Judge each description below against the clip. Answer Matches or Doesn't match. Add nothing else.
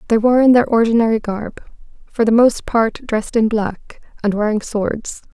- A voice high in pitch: Matches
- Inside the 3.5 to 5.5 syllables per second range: Matches